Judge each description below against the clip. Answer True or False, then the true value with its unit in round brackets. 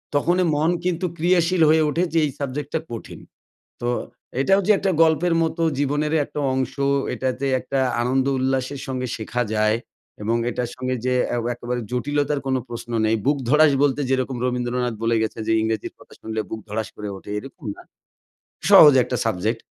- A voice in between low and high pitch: False (130 Hz)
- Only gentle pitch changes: False (4.0 semitones)